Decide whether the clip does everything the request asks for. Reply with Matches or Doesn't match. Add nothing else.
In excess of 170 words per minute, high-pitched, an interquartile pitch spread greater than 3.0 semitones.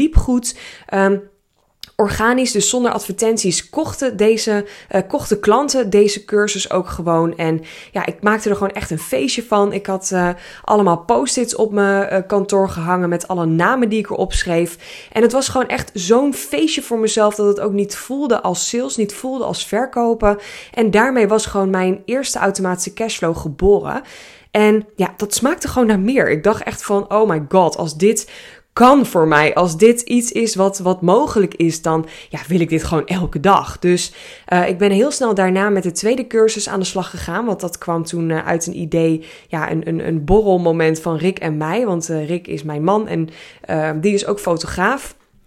Matches